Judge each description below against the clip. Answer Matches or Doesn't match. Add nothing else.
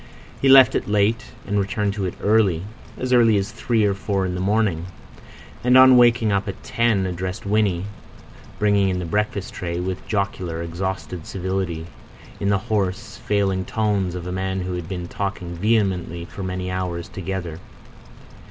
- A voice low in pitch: Matches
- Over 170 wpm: Doesn't match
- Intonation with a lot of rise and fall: Doesn't match